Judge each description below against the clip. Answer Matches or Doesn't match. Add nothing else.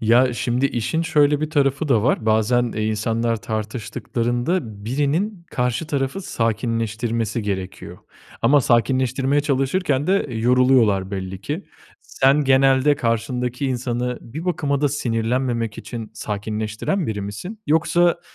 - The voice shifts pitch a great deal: Doesn't match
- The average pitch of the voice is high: Doesn't match